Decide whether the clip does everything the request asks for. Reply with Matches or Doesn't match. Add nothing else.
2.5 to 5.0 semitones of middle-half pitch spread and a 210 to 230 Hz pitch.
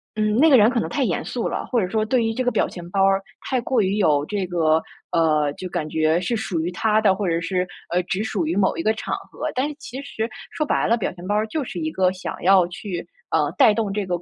Doesn't match